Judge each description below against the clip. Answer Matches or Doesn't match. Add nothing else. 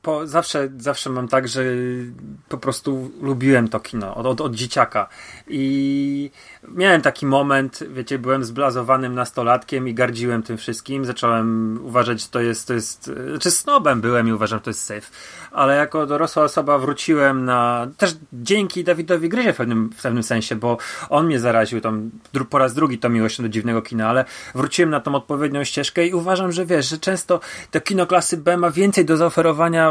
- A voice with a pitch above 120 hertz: Matches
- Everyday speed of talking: Doesn't match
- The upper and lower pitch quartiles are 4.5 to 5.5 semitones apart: Matches